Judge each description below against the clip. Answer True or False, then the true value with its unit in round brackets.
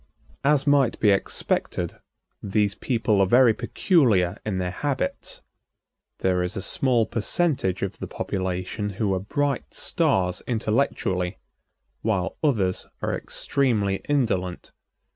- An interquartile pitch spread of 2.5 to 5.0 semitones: False (5.5 semitones)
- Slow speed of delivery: True (120 wpm)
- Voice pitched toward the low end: True (105 Hz)